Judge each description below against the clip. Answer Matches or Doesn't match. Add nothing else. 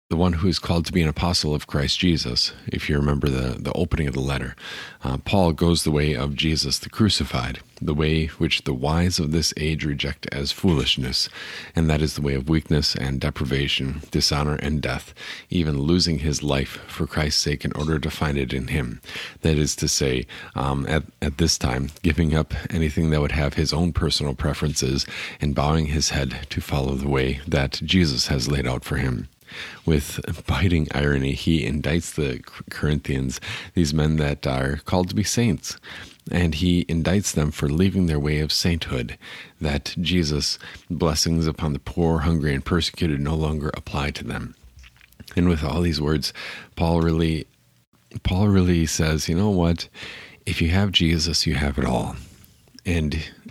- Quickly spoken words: Doesn't match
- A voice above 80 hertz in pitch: Doesn't match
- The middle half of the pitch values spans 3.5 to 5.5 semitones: Doesn't match